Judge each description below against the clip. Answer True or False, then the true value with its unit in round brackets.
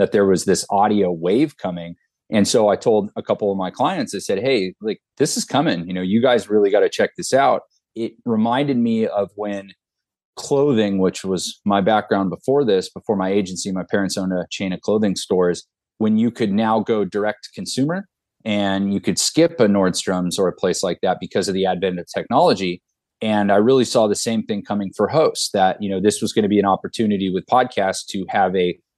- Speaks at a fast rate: True (220 wpm)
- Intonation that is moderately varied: True (3.0 semitones)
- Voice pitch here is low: True (100 Hz)